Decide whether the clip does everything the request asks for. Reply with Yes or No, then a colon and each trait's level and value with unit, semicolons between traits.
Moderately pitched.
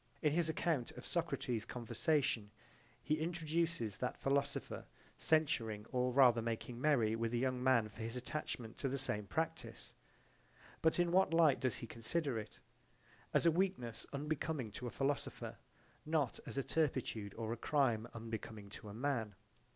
No: low, 130 Hz